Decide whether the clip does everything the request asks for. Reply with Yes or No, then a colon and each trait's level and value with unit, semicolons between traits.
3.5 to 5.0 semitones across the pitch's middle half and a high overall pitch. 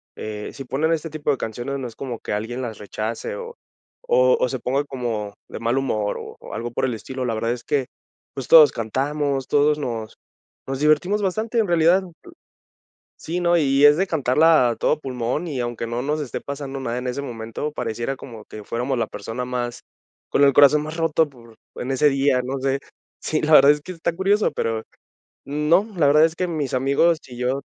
No: average, 4.2 semitones; low, 135 Hz